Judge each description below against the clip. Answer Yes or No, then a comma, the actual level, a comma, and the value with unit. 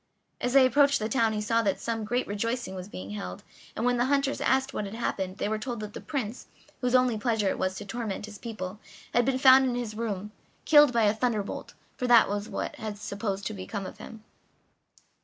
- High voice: Yes, high, 225 Hz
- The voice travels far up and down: No, average, 3.2 semitones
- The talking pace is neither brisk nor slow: No, fast, 230 wpm